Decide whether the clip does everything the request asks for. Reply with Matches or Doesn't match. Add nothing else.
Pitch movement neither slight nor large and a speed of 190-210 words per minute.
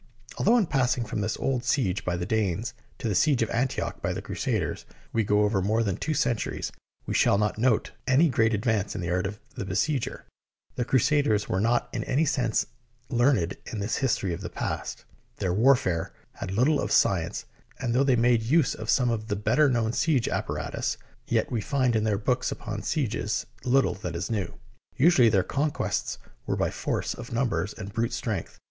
Matches